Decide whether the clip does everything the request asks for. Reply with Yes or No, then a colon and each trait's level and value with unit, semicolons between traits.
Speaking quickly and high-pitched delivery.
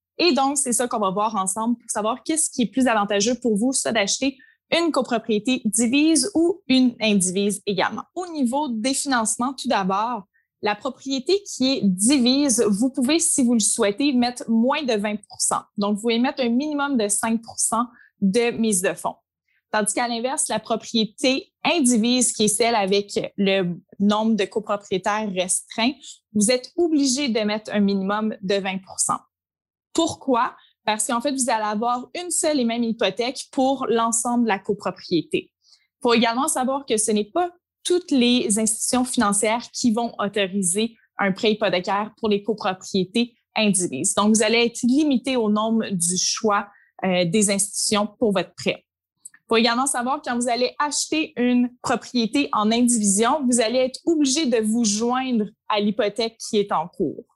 No: average, 170 wpm; high, 235 Hz